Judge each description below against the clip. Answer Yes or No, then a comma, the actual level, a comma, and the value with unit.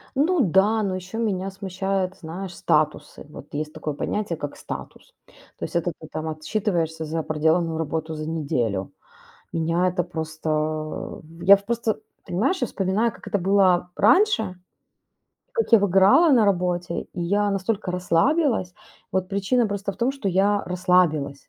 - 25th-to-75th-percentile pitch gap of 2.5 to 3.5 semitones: No, average, 4.1 semitones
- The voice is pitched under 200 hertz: Yes, medium, 185 Hz